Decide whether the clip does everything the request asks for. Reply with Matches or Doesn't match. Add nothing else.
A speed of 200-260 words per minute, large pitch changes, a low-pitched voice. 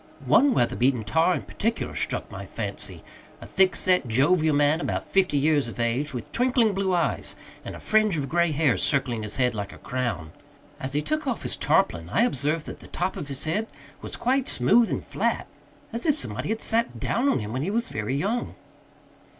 Doesn't match